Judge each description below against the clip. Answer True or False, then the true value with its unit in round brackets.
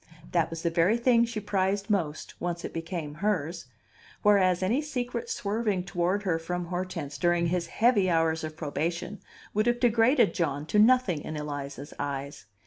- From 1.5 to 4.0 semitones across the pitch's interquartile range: False (4.5 semitones)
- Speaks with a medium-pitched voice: True (180 Hz)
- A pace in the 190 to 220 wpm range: False (165 wpm)